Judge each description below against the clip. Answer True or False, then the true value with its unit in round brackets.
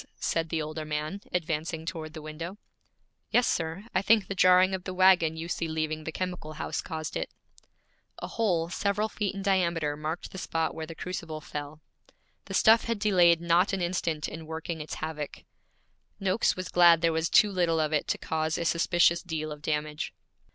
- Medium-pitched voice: True (165 Hz)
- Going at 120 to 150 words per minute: False (190 wpm)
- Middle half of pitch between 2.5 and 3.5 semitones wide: True (2.9 semitones)